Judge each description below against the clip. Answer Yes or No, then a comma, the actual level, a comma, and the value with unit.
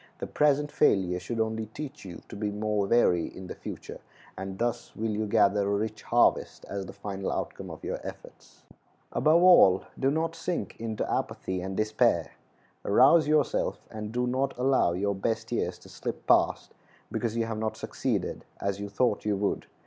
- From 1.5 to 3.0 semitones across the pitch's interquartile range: No, average, 3.9 semitones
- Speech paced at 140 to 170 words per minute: No, average, 180 wpm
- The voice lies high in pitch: No, low, 110 Hz